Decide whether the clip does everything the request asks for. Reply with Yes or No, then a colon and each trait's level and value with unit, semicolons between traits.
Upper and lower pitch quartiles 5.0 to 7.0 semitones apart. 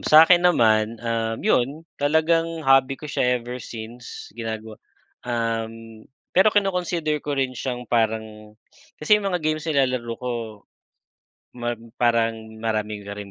Yes: average, 5.3 semitones